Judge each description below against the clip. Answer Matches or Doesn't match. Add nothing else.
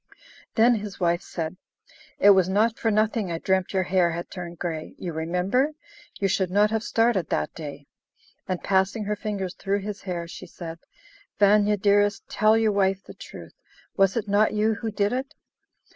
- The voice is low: Doesn't match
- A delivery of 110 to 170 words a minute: Doesn't match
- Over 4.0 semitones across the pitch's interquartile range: Doesn't match